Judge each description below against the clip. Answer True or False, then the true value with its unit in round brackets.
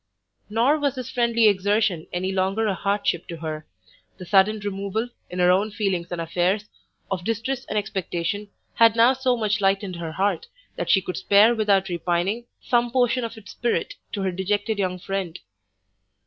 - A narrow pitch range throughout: False (3.6 semitones)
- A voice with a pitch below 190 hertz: False (200 Hz)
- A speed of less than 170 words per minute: False (175 wpm)